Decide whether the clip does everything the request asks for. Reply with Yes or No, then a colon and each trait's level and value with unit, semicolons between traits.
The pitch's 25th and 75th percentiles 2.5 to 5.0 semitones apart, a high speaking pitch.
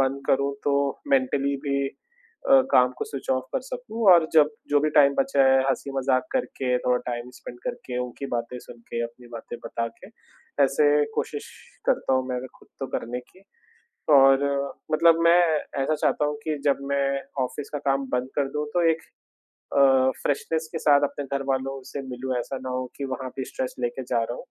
No: average, 3.0 semitones; medium, 140 Hz